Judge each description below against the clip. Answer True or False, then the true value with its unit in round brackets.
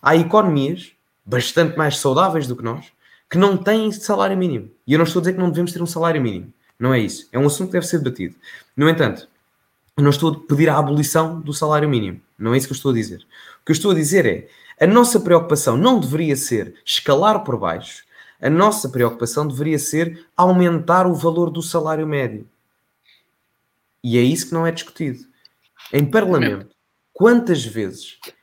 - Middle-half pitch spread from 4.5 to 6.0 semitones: True (5.2 semitones)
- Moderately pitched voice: True (155 Hz)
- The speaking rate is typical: False (195 wpm)